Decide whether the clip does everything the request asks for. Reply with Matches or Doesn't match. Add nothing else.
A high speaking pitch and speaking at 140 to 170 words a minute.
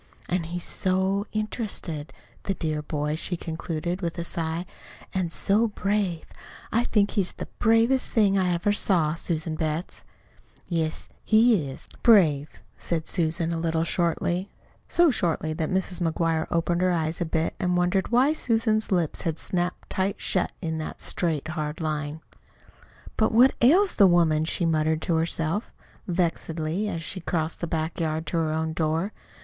Doesn't match